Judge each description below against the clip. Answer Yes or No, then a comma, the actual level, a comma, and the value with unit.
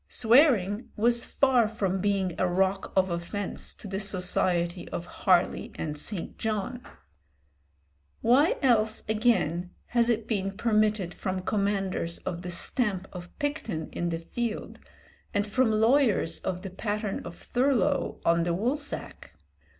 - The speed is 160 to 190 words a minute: No, slow, 135 wpm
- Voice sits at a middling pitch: No, high, 205 Hz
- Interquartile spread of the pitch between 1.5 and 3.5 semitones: No, average, 4.4 semitones